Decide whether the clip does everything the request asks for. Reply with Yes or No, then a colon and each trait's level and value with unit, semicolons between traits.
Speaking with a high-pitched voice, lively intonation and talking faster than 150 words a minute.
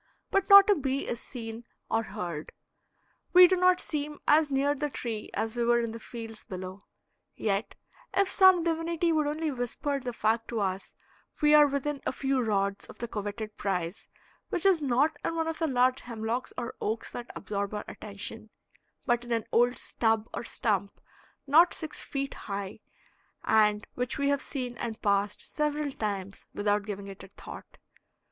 Yes: high, 240 Hz; wide, 5.8 semitones; average, 180 wpm